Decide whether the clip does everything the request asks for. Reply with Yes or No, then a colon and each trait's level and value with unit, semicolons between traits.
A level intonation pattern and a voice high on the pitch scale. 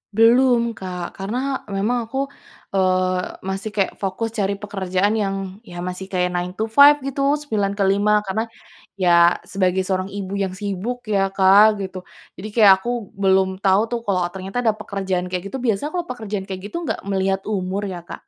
Yes: narrow, 2.3 semitones; high, 195 Hz